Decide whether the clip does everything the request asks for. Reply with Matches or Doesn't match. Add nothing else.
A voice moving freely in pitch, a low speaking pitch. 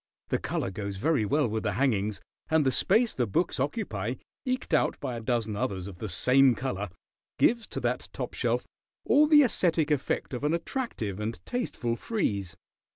Matches